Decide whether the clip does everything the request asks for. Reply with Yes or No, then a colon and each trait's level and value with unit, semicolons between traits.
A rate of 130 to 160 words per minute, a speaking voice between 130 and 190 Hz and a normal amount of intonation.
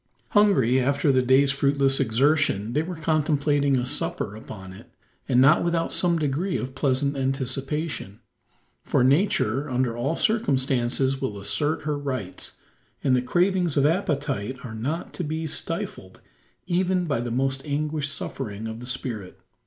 Yes: average, 150 wpm; medium, 140 Hz; average, 3.7 semitones